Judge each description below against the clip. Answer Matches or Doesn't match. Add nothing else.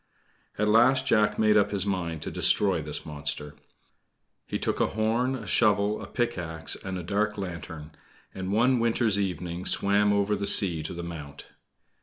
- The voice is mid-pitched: Doesn't match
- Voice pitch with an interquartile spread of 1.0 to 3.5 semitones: Doesn't match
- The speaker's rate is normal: Matches